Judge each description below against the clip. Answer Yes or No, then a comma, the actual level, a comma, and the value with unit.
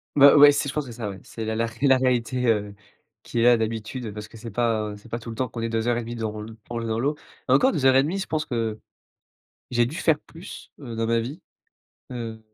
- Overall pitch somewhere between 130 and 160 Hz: No, low, 115 Hz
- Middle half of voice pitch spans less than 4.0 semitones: Yes, average, 2.9 semitones